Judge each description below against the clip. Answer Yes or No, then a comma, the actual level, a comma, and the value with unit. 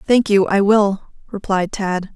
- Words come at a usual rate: Yes, average, 165 wpm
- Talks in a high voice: Yes, high, 200 Hz